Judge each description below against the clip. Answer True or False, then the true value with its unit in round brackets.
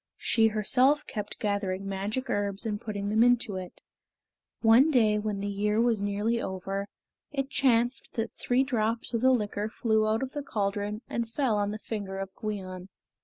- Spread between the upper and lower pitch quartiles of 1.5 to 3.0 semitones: True (2.7 semitones)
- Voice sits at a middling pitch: False (215 Hz)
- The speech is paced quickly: False (175 wpm)